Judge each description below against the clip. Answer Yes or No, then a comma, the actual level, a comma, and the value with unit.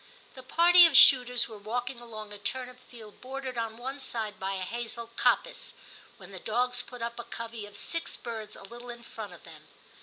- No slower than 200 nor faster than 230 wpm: Yes, fast, 205 wpm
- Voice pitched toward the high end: Yes, high, 235 Hz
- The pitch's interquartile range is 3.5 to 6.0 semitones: No, narrow, 2.5 semitones